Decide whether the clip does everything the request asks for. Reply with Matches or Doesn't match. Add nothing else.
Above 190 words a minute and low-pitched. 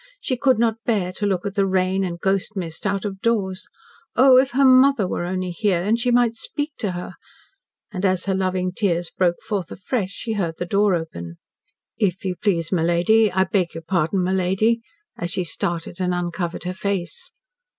Doesn't match